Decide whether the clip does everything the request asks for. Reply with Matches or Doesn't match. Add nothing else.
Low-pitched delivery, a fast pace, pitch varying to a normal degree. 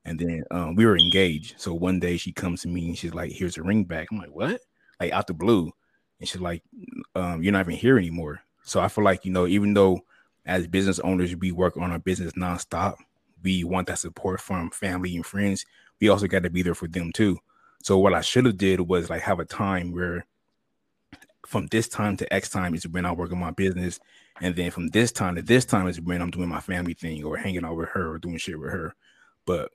Doesn't match